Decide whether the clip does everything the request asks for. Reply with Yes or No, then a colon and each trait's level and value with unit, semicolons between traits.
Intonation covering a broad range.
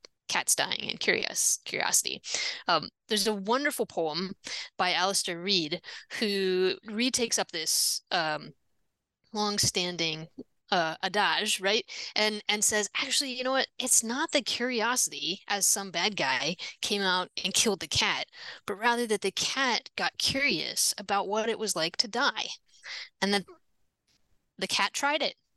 No: average, 3.7 semitones